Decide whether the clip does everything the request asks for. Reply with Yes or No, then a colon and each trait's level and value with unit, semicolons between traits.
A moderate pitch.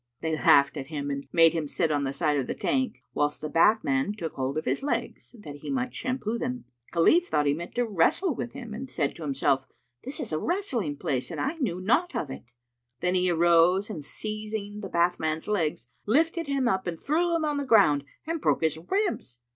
Yes: medium, 180 Hz